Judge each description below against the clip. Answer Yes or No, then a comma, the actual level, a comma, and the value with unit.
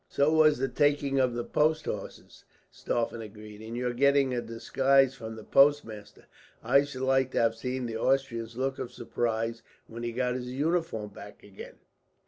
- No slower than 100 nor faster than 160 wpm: No, average, 175 wpm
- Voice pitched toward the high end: No, low, 125 Hz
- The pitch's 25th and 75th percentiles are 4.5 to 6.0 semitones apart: No, average, 3.2 semitones